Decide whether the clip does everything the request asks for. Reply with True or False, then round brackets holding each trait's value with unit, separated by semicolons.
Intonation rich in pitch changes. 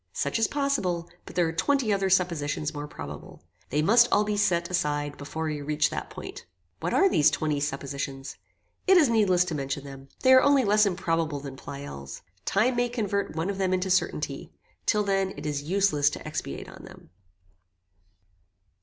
True (5.9 semitones)